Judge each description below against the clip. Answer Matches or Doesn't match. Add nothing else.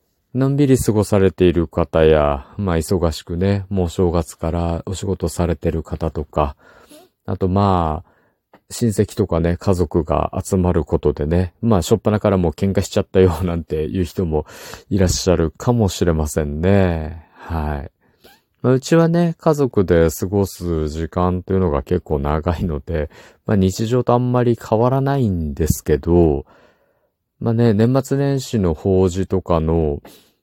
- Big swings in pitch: Doesn't match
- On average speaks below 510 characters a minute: Matches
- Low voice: Matches